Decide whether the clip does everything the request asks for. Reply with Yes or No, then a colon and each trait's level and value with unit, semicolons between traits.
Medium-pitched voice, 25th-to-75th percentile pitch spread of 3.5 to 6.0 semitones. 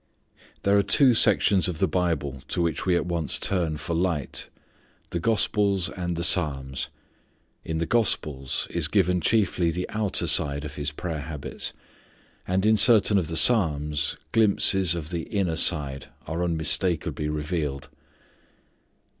No: very low, 85 Hz; average, 4.2 semitones